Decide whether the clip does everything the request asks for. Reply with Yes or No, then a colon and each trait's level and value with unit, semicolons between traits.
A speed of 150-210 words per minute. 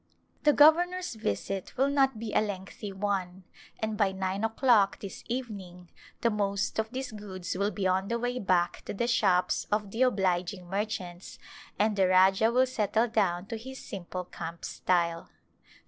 Yes: average, 165 wpm